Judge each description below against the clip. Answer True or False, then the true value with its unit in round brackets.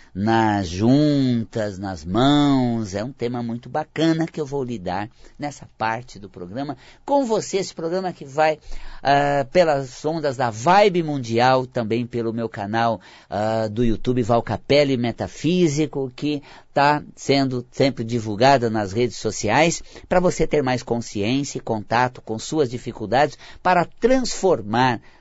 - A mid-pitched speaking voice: False (130 Hz)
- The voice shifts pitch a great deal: False (4.8 semitones)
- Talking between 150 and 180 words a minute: False (140 wpm)